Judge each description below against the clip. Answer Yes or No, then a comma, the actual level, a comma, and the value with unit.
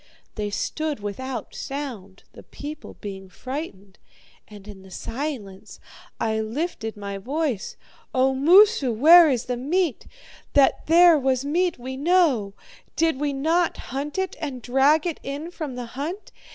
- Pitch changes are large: Yes, wide, 6.1 semitones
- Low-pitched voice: No, very high, 270 Hz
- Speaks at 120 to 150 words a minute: Yes, average, 145 wpm